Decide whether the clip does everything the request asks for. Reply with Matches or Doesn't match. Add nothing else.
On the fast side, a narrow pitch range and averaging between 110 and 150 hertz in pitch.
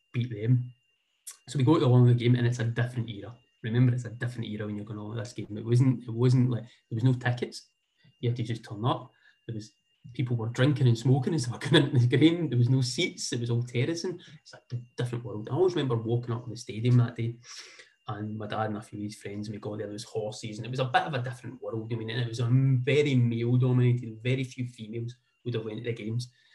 Matches